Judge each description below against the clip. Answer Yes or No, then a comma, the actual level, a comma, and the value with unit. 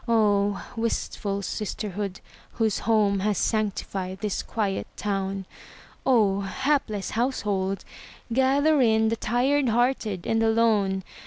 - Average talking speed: No, slow, 110 wpm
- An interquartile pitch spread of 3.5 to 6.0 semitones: No, average, 2.8 semitones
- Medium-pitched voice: No, high, 215 Hz